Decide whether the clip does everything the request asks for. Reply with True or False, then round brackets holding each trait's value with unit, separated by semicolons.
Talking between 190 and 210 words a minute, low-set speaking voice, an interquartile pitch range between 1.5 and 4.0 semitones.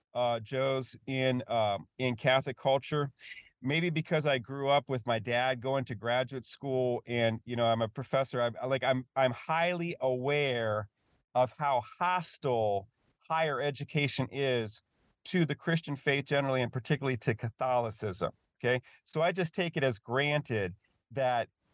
False (150 wpm; 130 Hz; 3.0 semitones)